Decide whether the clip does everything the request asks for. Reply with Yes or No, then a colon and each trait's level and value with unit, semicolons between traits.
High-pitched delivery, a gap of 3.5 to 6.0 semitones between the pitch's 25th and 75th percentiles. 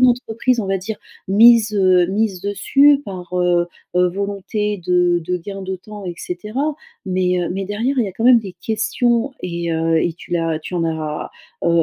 Yes: high, 195 Hz; average, 3.8 semitones